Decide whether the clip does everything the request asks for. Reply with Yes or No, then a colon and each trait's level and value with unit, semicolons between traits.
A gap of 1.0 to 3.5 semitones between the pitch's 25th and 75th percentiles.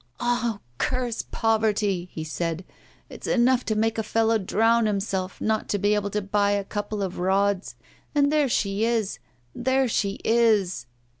Yes: narrow, 2.6 semitones